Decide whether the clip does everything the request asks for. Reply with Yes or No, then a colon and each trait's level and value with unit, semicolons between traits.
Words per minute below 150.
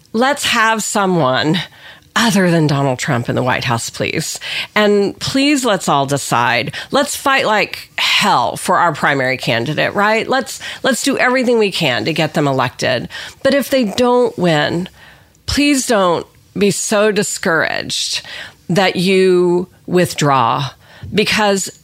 Yes: slow, 135 wpm